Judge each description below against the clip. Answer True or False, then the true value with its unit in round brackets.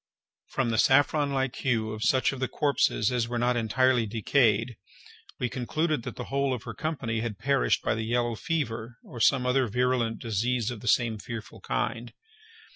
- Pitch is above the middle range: False (120 Hz)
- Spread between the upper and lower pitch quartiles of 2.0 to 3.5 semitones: True (2.7 semitones)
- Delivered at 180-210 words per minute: True (185 wpm)